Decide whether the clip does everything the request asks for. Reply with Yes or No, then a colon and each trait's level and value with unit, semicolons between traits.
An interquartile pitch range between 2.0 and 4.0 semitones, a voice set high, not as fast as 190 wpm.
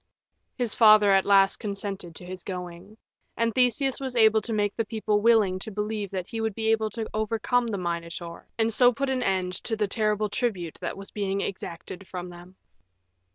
No: average, 3.0 semitones; high, 210 Hz; average, 195 wpm